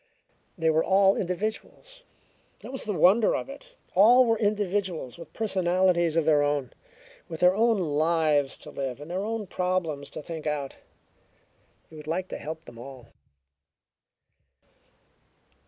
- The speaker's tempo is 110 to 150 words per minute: Yes, average, 145 wpm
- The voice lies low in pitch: No, medium, 175 Hz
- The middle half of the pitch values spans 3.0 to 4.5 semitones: No, average, 5.0 semitones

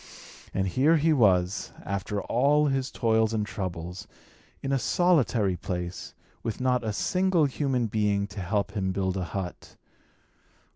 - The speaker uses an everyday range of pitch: No, wide, 5.9 semitones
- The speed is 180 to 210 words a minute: No, average, 145 wpm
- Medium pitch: No, low, 110 Hz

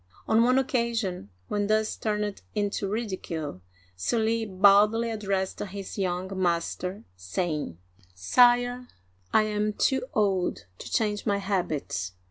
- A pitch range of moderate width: Yes, average, 3.4 semitones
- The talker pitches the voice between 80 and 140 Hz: No, high, 205 Hz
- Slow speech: Yes, slow, 120 wpm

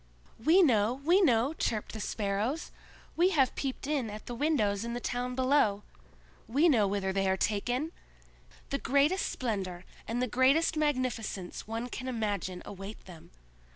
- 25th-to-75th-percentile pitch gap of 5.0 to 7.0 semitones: Yes, average, 5.3 semitones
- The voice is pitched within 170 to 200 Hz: No, high, 240 Hz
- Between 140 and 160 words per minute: Yes, average, 155 wpm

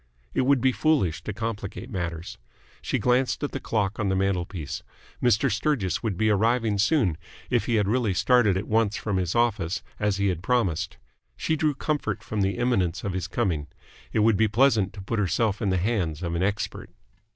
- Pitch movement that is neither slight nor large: Yes, average, 4.0 semitones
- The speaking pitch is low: Yes, low, 105 Hz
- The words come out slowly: No, average, 195 wpm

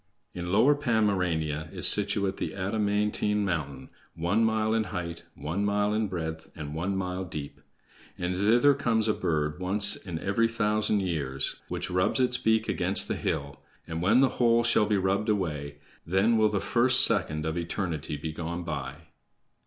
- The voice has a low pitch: Yes, very low, 95 Hz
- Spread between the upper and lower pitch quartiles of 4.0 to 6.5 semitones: Yes, average, 4.8 semitones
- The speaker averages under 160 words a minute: No, average, 170 wpm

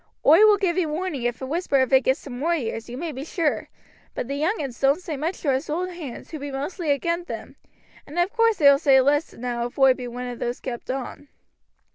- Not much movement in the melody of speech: No, average, 4.5 semitones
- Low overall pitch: No, very high, 285 Hz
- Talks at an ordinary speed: No, fast, 250 wpm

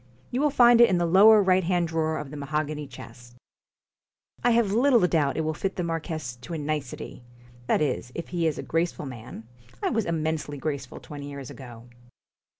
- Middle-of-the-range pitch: Yes, medium, 160 Hz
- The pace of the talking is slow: No, average, 195 wpm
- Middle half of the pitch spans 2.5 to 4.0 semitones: No, average, 4.5 semitones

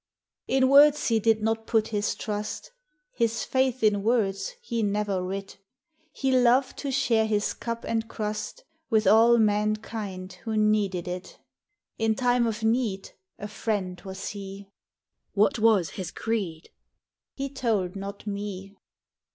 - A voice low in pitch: No, high, 215 Hz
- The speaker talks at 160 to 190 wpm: No, average, 150 wpm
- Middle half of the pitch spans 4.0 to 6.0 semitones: No, narrow, 2.5 semitones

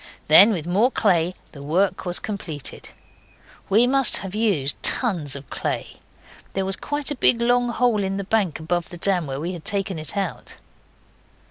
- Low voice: No, high, 195 Hz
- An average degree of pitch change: Yes, average, 4.8 semitones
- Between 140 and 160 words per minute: No, average, 175 wpm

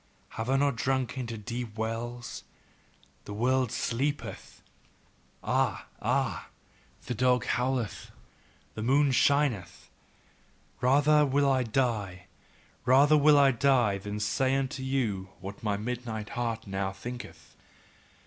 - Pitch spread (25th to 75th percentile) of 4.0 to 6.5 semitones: No, average, 3.5 semitones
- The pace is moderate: No, slow, 120 wpm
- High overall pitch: No, low, 125 Hz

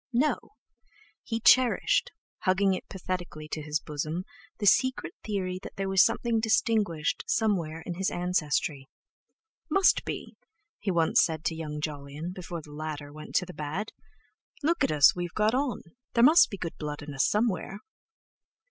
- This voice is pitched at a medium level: Yes, medium, 180 Hz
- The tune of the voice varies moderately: No, wide, 5.7 semitones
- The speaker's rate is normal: Yes, average, 160 wpm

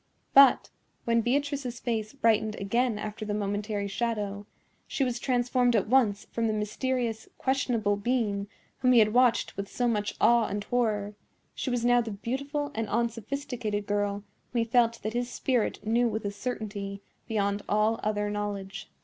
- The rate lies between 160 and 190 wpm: Yes, average, 165 wpm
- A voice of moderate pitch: No, high, 225 Hz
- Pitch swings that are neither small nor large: Yes, average, 3.0 semitones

